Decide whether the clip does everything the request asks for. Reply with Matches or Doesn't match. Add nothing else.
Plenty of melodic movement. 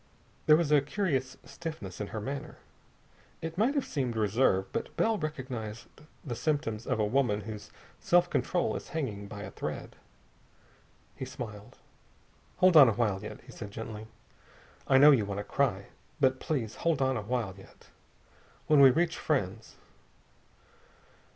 Matches